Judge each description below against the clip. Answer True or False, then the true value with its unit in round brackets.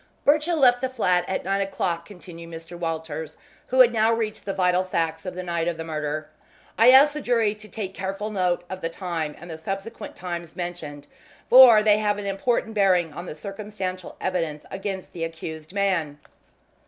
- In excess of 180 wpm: True (190 wpm)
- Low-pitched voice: False (185 Hz)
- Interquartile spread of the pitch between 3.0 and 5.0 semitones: True (4.2 semitones)